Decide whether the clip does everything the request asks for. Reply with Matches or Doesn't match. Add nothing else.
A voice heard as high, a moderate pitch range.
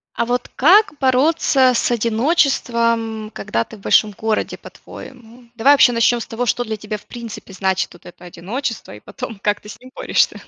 Matches